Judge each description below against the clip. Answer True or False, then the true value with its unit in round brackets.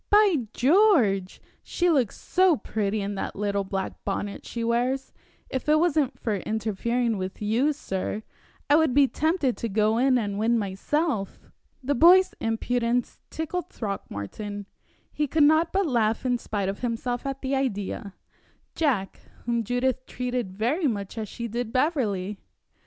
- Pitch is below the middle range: False (240 Hz)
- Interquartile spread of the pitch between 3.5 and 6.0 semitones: True (5.5 semitones)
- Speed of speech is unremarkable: True (150 wpm)